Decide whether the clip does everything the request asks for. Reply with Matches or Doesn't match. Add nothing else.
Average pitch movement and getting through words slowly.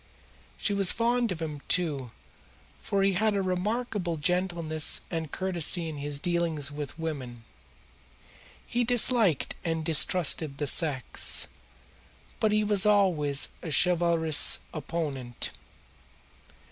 Matches